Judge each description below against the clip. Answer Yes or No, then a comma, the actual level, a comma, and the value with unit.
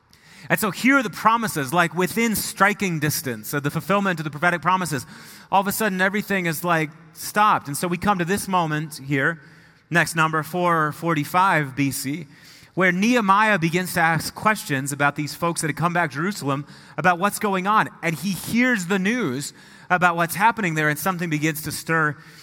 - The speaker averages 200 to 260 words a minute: No, average, 185 wpm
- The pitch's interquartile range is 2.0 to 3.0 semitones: No, average, 4.2 semitones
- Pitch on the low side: No, medium, 170 Hz